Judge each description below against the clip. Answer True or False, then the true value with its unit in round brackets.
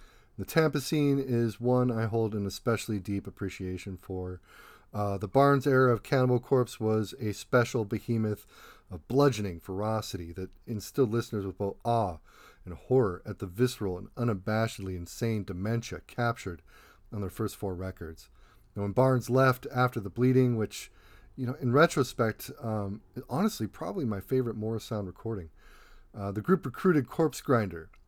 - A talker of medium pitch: False (110 Hz)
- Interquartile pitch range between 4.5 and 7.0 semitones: False (4.1 semitones)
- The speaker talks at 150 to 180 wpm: True (155 wpm)